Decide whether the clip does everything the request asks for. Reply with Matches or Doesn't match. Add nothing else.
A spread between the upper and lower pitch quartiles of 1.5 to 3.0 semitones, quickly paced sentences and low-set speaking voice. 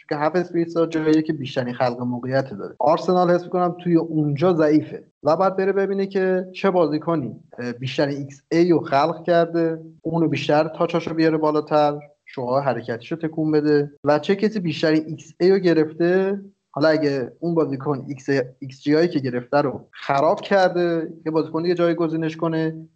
Doesn't match